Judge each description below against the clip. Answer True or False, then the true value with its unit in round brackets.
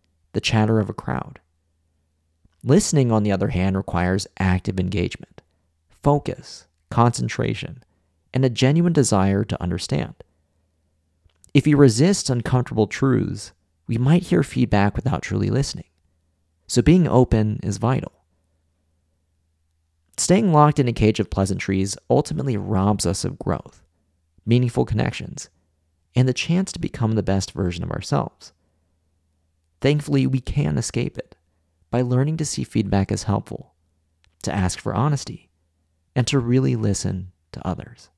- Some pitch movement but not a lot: False (7.5 semitones)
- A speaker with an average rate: False (130 wpm)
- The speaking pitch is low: True (95 Hz)